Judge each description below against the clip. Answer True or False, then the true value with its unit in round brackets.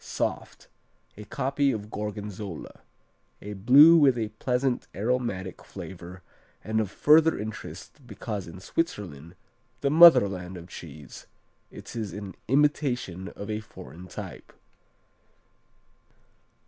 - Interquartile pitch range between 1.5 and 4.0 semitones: False (5.6 semitones)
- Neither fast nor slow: False (110 wpm)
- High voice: False (105 Hz)